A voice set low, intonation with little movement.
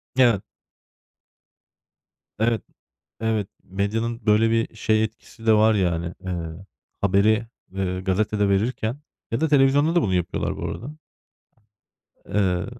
No: low, 110 Hz; average, 3.0 semitones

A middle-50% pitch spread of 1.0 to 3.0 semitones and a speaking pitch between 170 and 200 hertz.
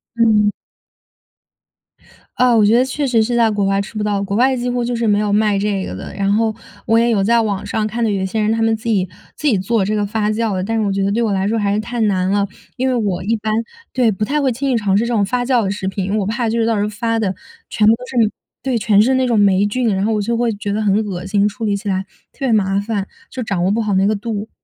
No: narrow, 2.5 semitones; high, 215 Hz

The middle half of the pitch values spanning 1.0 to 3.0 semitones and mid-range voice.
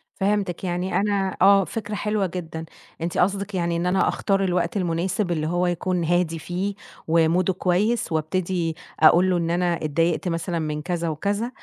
Yes: narrow, 2.5 semitones; medium, 180 Hz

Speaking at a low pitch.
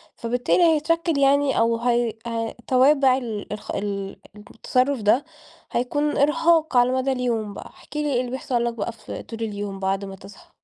No: high, 245 Hz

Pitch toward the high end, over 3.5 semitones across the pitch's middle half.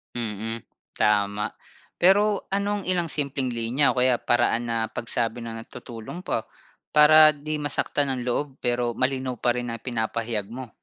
No: low, 125 Hz; average, 4.2 semitones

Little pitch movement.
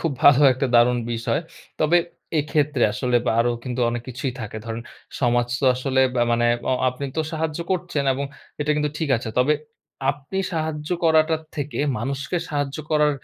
No: average, 3.8 semitones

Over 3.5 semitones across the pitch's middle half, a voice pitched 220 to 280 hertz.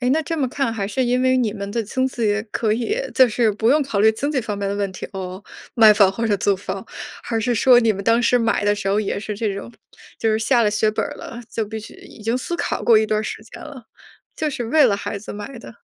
No: average, 3.2 semitones; high, 225 Hz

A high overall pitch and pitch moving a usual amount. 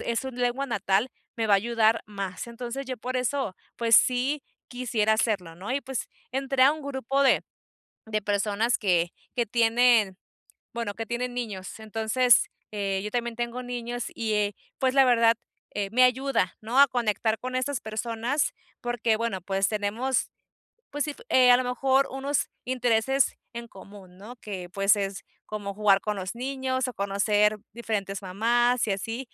Yes: high, 230 Hz; average, 3.4 semitones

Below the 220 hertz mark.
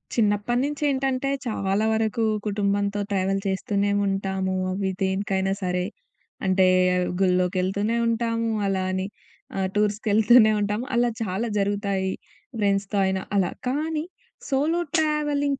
Yes: high, 205 Hz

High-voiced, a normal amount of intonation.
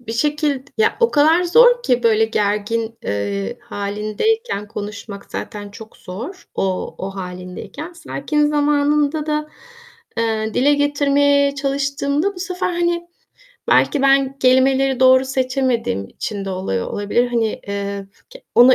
No: very high, 260 Hz; wide, 6.1 semitones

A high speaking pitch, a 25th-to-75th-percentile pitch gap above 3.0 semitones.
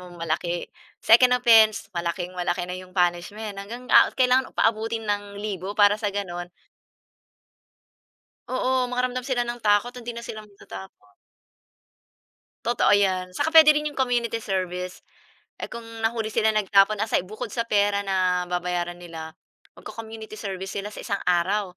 Yes: high, 205 Hz; average, 4.1 semitones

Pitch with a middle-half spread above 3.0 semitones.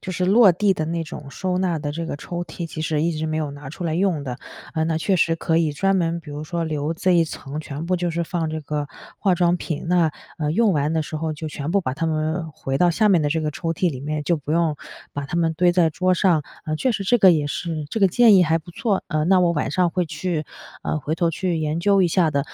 No: average, 2.7 semitones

